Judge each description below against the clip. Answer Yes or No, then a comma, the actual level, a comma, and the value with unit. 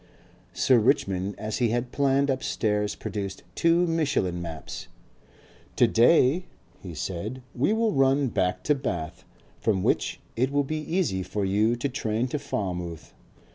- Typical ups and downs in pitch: No, wide, 6.5 semitones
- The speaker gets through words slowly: No, average, 145 wpm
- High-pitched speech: No, low, 120 Hz